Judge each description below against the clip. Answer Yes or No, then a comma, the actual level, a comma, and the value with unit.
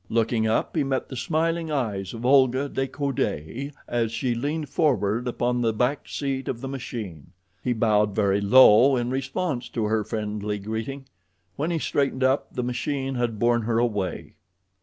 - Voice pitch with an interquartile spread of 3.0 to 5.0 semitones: Yes, average, 3.6 semitones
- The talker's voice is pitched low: Yes, low, 120 Hz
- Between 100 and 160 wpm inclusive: No, average, 170 wpm